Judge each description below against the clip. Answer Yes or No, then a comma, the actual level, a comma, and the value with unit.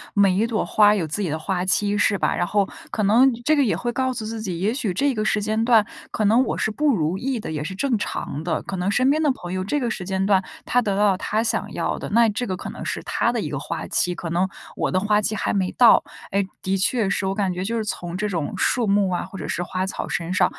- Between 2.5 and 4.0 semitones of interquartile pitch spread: Yes, average, 3.4 semitones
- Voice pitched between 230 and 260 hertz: No, high, 205 Hz